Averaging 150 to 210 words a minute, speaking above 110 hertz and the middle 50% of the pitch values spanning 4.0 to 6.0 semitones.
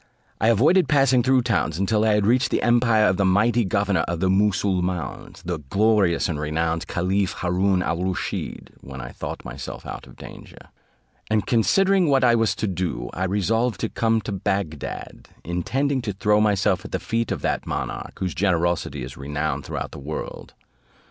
No: average, 180 wpm; low, 100 Hz; average, 4.6 semitones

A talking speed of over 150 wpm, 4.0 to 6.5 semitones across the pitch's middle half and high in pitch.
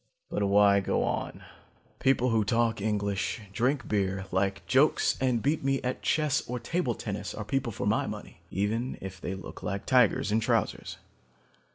No: average, 170 wpm; average, 4.3 semitones; low, 115 Hz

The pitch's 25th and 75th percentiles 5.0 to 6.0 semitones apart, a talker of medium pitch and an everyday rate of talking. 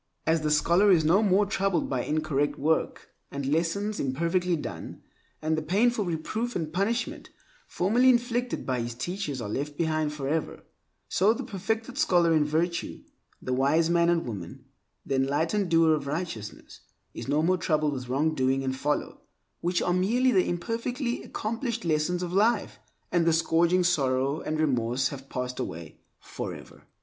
Yes: average, 5.3 semitones; medium, 165 Hz; average, 165 wpm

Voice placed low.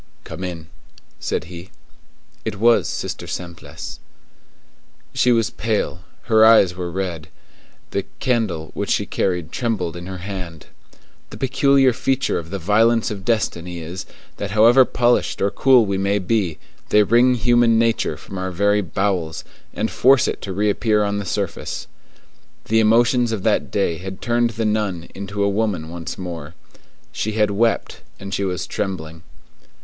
Yes: low, 100 Hz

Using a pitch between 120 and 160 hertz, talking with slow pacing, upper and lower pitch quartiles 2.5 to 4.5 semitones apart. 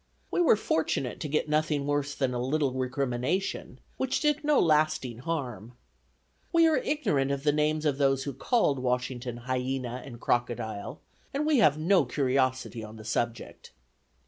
No: medium, 140 Hz; average, 160 wpm; average, 3.7 semitones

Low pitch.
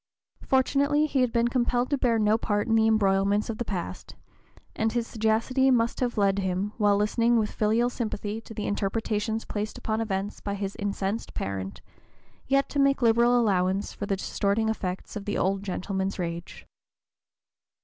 No: high, 215 Hz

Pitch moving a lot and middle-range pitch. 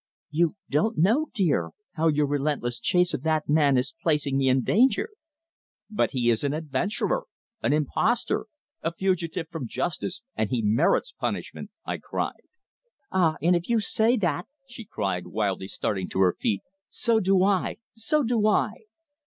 Yes: wide, 7.4 semitones; medium, 160 Hz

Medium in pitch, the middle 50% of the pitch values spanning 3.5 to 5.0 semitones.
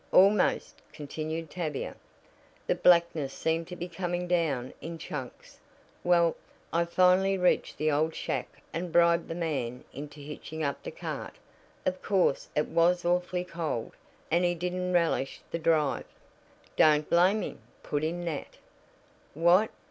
No: medium, 170 Hz; narrow, 2.5 semitones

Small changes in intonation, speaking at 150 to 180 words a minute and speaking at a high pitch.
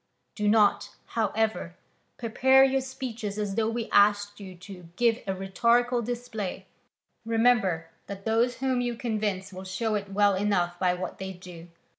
No: average, 3.6 semitones; average, 155 wpm; high, 210 Hz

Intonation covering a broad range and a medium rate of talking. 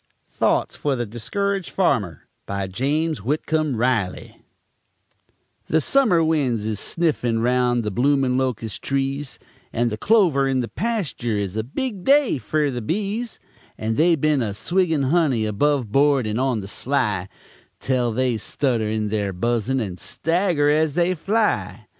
Yes: wide, 6.2 semitones; average, 150 wpm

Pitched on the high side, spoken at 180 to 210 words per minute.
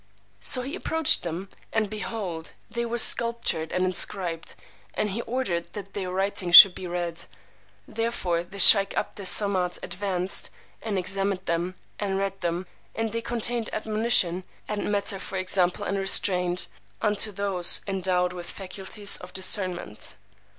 No: high, 195 Hz; average, 145 wpm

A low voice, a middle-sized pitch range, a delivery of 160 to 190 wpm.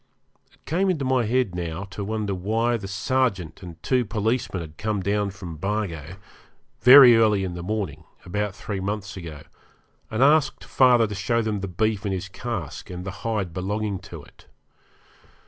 Yes: low, 105 Hz; average, 3.7 semitones; average, 175 wpm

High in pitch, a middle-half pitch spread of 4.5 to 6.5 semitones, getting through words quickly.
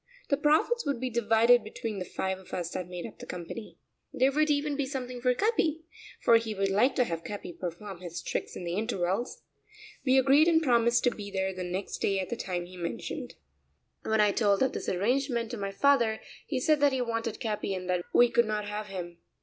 Yes: high, 225 Hz; average, 5.3 semitones; fast, 220 wpm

